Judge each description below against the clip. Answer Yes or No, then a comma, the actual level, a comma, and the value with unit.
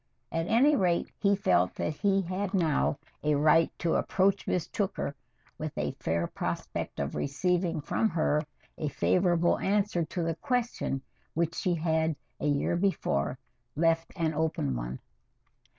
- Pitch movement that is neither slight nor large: Yes, average, 3.9 semitones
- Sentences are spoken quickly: No, average, 150 wpm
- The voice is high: No, medium, 165 Hz